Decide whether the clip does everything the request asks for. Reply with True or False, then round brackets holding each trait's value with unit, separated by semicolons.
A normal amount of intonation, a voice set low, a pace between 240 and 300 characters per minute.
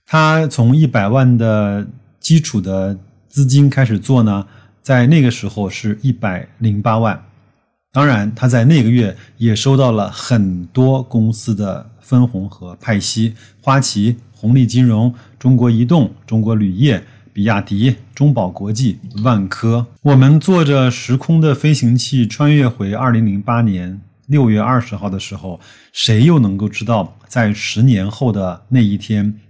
False (3.7 semitones; 115 Hz; 225 characters per minute)